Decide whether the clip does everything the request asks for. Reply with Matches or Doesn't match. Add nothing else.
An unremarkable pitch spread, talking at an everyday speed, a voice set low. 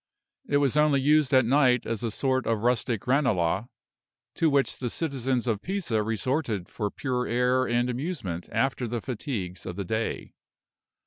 Matches